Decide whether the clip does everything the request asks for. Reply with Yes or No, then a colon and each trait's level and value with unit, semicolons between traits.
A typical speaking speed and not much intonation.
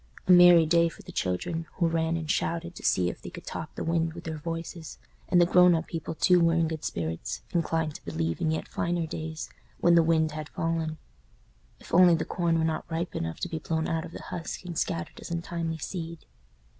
No: fast, 225 wpm; narrow, 1.2 semitones